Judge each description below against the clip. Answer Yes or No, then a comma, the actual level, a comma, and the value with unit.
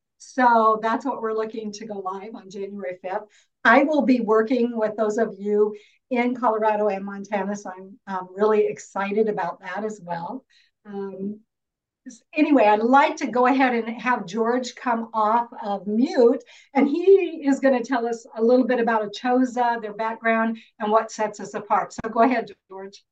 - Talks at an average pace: Yes, average, 180 wpm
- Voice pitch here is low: No, high, 225 Hz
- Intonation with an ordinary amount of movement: Yes, average, 3.0 semitones